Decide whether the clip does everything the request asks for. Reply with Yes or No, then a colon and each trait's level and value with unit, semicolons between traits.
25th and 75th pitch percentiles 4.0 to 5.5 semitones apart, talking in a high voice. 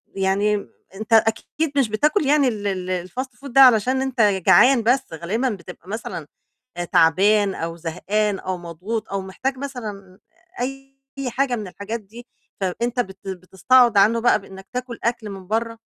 Yes: average, 4.3 semitones; high, 215 Hz